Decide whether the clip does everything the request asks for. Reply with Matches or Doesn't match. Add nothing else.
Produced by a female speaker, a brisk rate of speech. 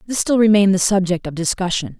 Matches